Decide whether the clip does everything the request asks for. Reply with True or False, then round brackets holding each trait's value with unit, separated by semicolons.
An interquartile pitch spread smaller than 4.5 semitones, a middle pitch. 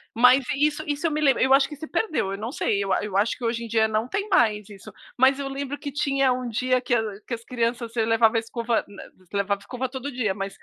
False (3.7 semitones; 245 Hz)